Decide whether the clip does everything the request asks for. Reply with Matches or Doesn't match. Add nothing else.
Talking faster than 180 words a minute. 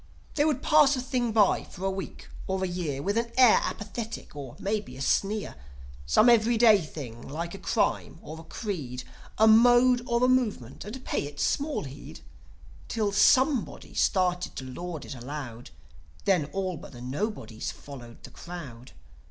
Doesn't match